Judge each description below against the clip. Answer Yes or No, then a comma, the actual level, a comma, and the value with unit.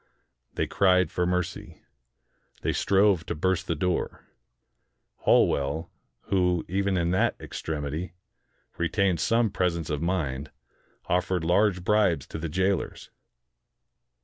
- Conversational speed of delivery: No, slow, 120 wpm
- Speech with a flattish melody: Yes, narrow, 2.3 semitones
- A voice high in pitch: No, very low, 90 Hz